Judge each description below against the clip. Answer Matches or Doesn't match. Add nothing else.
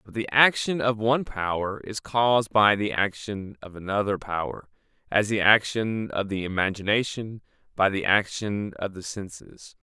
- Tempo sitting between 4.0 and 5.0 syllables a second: Matches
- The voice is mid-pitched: Doesn't match